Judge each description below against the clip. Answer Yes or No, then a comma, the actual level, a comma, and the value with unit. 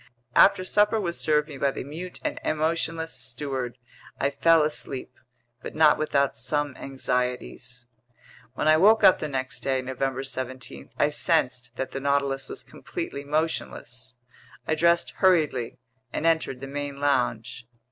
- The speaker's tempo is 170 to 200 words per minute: No, average, 145 wpm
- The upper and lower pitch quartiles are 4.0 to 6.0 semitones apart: No, average, 3.4 semitones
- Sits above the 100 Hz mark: Yes, medium, 140 Hz